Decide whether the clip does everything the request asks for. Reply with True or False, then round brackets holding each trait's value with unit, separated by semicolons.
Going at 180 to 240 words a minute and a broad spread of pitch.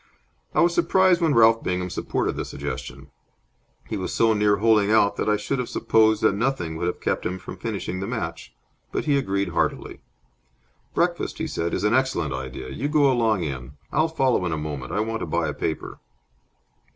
True (200 wpm; 6.7 semitones)